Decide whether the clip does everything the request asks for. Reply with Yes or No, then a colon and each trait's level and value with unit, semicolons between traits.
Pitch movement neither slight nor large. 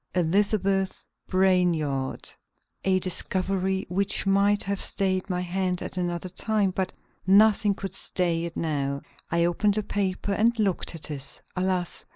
No: narrow, 2.1 semitones